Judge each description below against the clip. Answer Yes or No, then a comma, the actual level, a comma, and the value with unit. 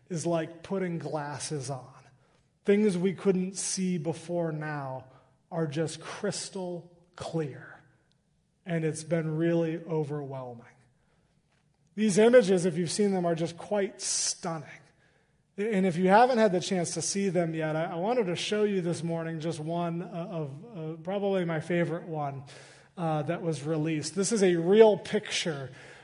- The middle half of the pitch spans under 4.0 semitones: Yes, average, 3.0 semitones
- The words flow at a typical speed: Yes, average, 150 wpm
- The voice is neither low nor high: Yes, medium, 165 Hz